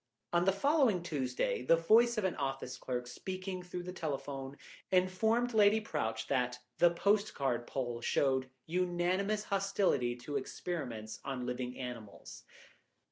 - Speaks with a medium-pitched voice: Yes, medium, 165 Hz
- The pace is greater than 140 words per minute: No, slow, 135 wpm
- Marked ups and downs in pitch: Yes, wide, 7.3 semitones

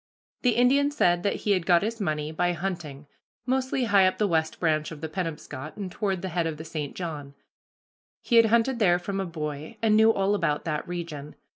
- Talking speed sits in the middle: No, fast, 210 wpm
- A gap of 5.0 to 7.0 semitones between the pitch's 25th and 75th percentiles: Yes, average, 5.3 semitones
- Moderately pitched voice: Yes, medium, 175 Hz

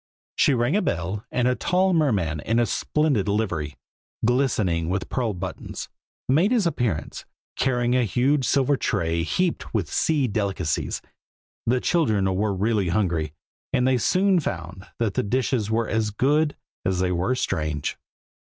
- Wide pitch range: Yes, wide, 6.1 semitones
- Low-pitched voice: Yes, low, 110 Hz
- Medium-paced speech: Yes, average, 155 wpm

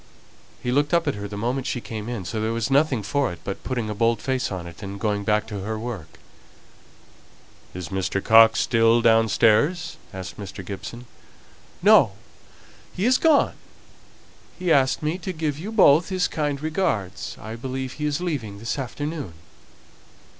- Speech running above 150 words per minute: Yes, average, 170 wpm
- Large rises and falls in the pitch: Yes, wide, 5.9 semitones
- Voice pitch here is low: Yes, low, 115 Hz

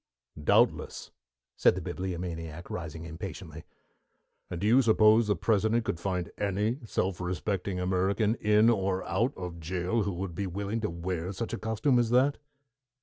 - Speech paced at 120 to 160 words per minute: Yes, average, 155 wpm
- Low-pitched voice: Yes, very low, 95 Hz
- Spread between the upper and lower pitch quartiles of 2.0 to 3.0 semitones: No, average, 3.7 semitones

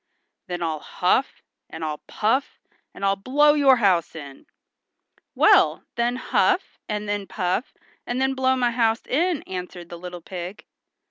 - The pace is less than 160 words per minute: Yes, average, 145 wpm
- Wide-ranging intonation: Yes, wide, 6.5 semitones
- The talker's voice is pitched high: Yes, high, 210 Hz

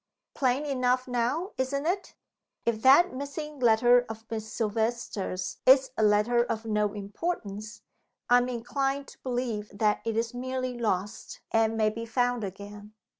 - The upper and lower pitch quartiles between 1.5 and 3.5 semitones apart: Yes, average, 3.1 semitones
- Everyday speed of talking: Yes, average, 150 wpm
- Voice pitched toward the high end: Yes, high, 235 Hz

